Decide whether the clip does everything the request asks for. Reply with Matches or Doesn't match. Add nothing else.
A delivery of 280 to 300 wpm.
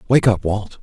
Doesn't match